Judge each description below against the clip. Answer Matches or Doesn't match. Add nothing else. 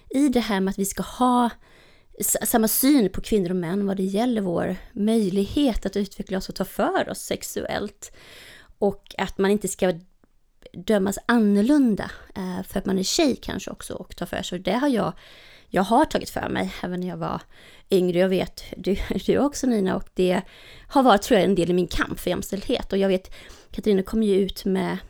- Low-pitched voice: Doesn't match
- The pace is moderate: Doesn't match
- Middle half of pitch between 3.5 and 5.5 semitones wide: Doesn't match